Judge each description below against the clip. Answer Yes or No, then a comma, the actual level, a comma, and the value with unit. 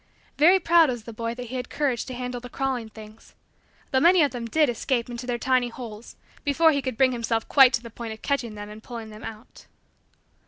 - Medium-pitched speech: No, high, 245 Hz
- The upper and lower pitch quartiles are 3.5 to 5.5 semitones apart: No, average, 2.7 semitones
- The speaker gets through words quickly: Yes, fast, 230 wpm